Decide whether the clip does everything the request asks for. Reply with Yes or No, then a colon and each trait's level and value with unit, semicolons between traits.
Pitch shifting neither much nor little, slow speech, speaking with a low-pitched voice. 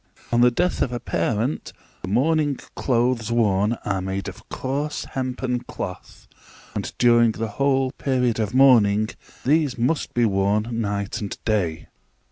No: average, 3.9 semitones; average, 145 wpm; low, 120 Hz